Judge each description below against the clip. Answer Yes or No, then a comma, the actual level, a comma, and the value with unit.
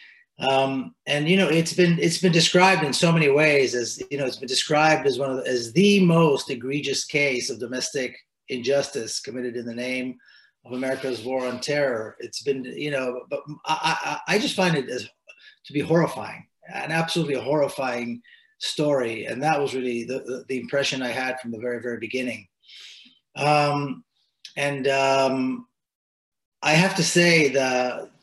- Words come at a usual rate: Yes, average, 170 wpm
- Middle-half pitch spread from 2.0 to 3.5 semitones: No, average, 3.9 semitones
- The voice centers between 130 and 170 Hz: Yes, medium, 140 Hz